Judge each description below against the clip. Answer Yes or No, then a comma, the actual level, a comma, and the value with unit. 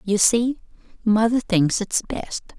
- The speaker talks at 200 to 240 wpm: No, average, 140 wpm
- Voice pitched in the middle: No, high, 215 Hz